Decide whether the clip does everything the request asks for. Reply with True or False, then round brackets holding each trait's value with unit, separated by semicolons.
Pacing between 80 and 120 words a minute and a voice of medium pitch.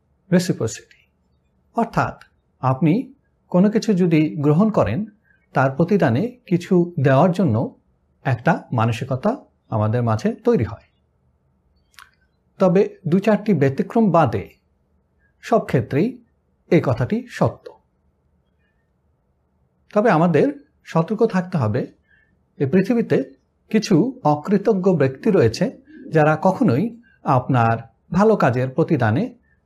True (90 wpm; 155 Hz)